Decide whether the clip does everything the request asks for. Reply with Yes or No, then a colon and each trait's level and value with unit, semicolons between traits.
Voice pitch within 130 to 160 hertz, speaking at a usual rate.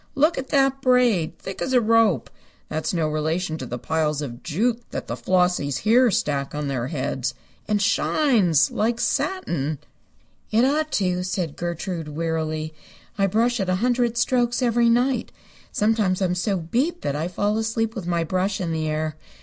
No: medium, 185 Hz; average, 175 wpm